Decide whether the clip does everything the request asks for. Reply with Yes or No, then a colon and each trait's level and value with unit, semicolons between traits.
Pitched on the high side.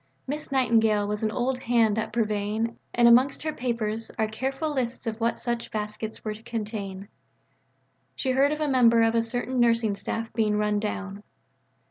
Yes: high, 230 Hz